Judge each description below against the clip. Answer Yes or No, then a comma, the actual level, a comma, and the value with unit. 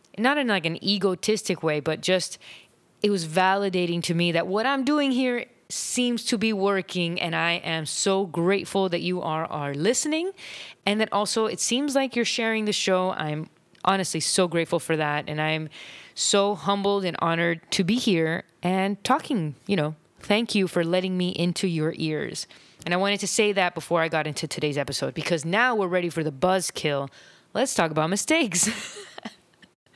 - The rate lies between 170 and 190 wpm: Yes, average, 185 wpm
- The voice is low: No, medium, 185 Hz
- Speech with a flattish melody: No, average, 4.0 semitones